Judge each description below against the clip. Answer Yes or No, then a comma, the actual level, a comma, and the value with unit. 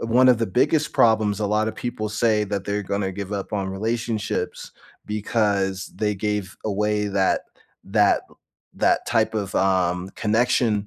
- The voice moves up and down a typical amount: No, narrow, 1.9 semitones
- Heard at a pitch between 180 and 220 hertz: No, low, 105 Hz